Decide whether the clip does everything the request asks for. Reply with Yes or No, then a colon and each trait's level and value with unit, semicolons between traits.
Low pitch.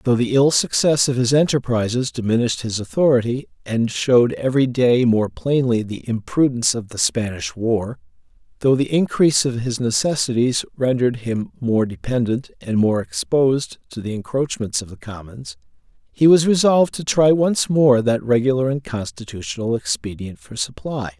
Yes: low, 125 Hz